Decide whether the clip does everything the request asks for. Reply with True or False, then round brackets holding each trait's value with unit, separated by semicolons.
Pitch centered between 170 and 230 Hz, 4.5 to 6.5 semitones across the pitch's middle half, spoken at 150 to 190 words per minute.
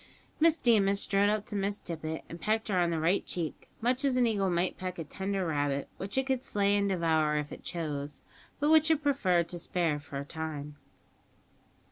False (185 Hz; 5.1 semitones; 205 wpm)